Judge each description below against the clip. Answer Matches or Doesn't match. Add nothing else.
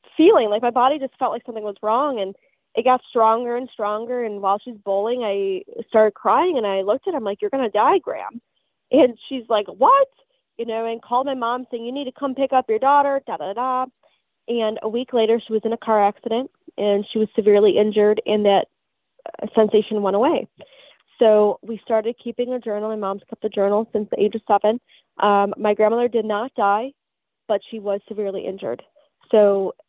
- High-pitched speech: Matches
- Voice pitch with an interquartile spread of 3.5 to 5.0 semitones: Doesn't match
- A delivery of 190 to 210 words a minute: Matches